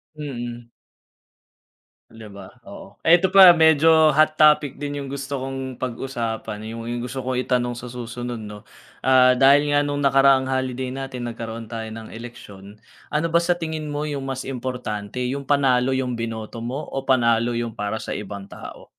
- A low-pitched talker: Yes, low, 130 Hz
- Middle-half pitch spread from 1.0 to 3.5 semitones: Yes, average, 3.2 semitones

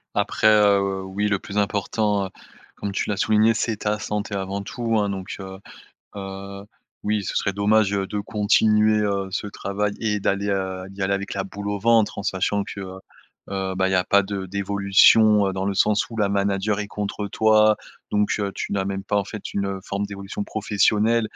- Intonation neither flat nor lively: No, narrow, 1.3 semitones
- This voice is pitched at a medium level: No, low, 100 Hz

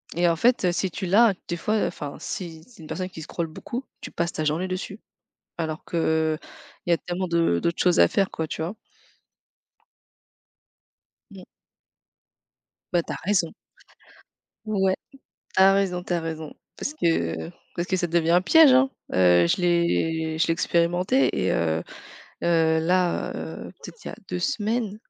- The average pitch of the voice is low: No, medium, 175 Hz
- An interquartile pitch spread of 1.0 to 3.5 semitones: Yes, average, 2.9 semitones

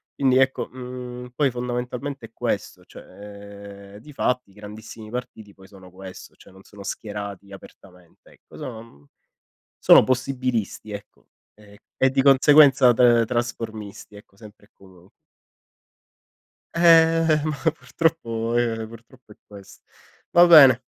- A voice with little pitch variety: No, average, 4.2 semitones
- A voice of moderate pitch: No, low, 115 Hz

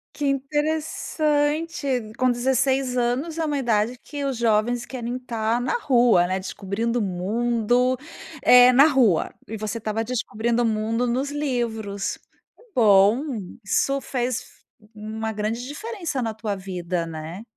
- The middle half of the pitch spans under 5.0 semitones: Yes, average, 3.7 semitones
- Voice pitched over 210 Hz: Yes, high, 240 Hz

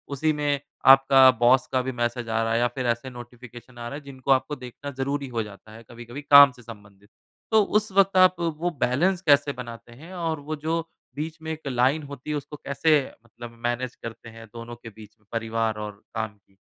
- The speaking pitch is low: Yes, low, 125 Hz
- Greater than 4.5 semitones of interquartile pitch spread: No, average, 3.9 semitones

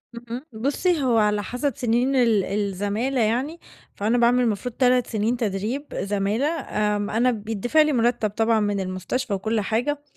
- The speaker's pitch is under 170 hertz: No, high, 230 Hz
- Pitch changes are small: No, average, 3.3 semitones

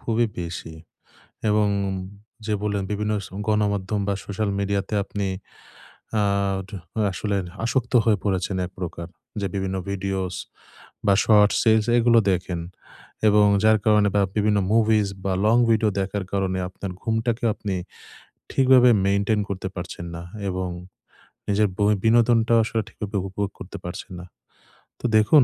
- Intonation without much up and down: Yes, narrow, 2.1 semitones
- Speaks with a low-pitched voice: Yes, low, 100 Hz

